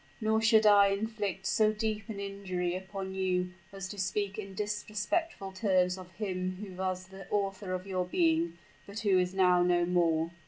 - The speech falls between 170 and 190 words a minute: Yes, average, 180 wpm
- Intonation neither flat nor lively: No, narrow, 2.3 semitones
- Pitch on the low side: No, high, 190 Hz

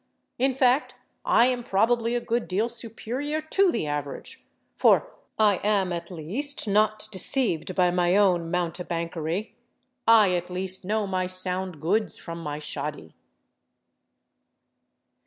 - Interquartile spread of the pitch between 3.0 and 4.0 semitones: No, average, 4.9 semitones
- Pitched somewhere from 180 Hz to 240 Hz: Yes, high, 190 Hz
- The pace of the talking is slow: Yes, slow, 125 wpm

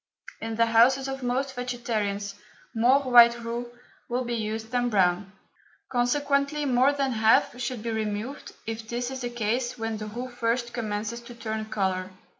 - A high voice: Yes, high, 235 Hz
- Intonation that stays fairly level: Yes, narrow, 2.2 semitones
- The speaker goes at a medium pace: Yes, average, 165 wpm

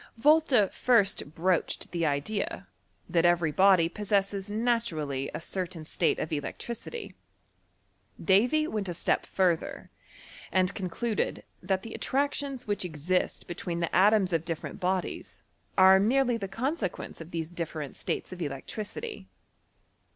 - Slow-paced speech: Yes, slow, 130 wpm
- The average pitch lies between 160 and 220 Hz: Yes, high, 190 Hz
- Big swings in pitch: No, average, 4.5 semitones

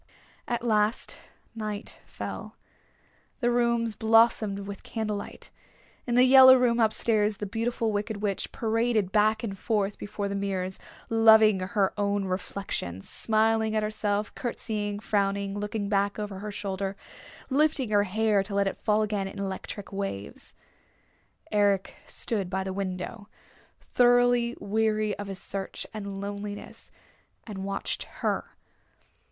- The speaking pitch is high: Yes, high, 210 Hz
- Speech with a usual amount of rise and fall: No, narrow, 2.0 semitones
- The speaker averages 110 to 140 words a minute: Yes, slow, 135 wpm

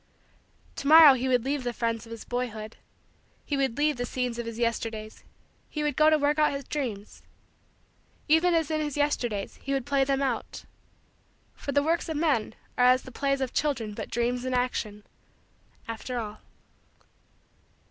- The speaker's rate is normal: Yes, average, 180 wpm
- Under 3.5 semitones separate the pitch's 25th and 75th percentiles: No, average, 3.9 semitones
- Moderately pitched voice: No, very high, 255 Hz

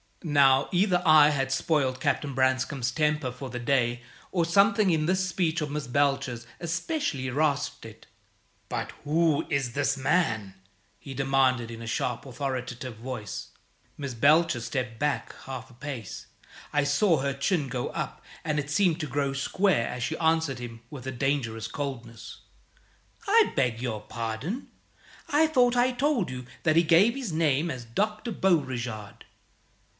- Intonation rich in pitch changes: No, average, 4.7 semitones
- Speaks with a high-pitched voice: No, medium, 140 Hz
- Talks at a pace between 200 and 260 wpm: No, average, 155 wpm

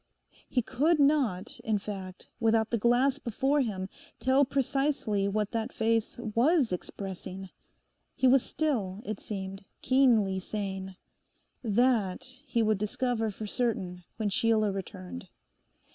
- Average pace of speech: No, slow, 125 wpm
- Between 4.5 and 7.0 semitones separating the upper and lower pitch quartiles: Yes, average, 4.8 semitones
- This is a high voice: Yes, high, 220 Hz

